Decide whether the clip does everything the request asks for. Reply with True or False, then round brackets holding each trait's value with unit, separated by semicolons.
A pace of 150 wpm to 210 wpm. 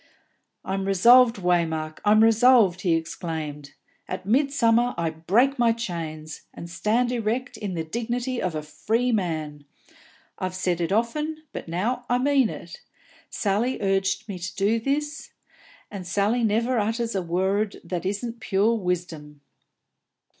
False (140 wpm)